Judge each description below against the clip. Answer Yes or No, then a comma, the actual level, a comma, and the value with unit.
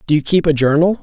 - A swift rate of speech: Yes, fast, 295 wpm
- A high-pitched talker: No, medium, 160 Hz